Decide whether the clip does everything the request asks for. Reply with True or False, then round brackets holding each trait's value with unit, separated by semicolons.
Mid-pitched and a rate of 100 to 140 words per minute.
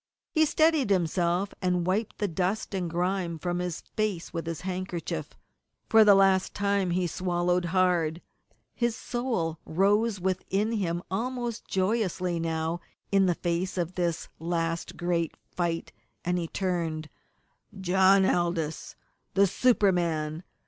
True (180 Hz; 135 wpm)